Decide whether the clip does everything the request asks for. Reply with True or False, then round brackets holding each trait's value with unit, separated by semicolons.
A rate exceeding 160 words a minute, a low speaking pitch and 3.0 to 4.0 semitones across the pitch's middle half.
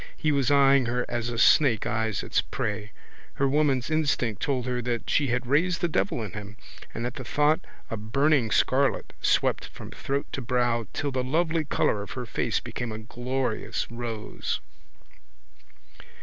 True (170 wpm; 125 Hz; 3.6 semitones)